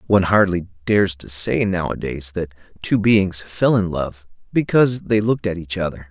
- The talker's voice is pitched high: No, very low, 95 Hz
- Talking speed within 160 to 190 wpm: Yes, average, 175 wpm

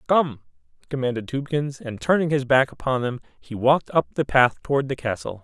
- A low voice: Yes, low, 130 Hz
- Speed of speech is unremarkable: Yes, average, 190 wpm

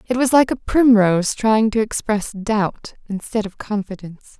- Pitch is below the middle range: No, high, 215 Hz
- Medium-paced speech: Yes, average, 165 wpm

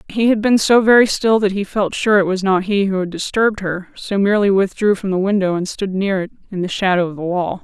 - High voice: Yes, high, 195 Hz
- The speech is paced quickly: Yes, fast, 265 wpm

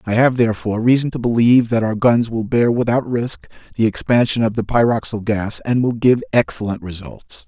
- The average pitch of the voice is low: Yes, low, 115 Hz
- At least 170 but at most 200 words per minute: Yes, average, 195 wpm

